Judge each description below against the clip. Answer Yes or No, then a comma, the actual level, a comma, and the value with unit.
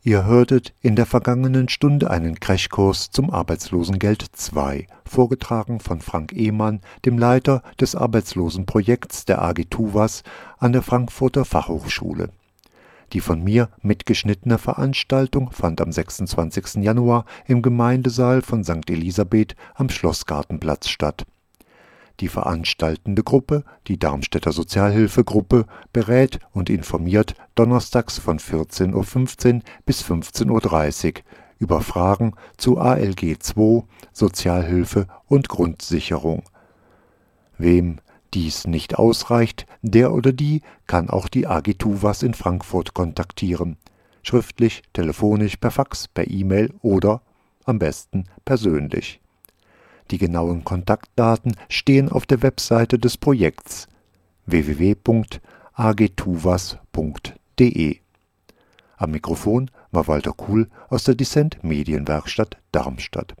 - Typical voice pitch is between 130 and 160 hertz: No, low, 105 Hz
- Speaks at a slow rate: Yes, slow, 105 wpm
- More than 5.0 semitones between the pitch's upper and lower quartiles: Yes, wide, 5.6 semitones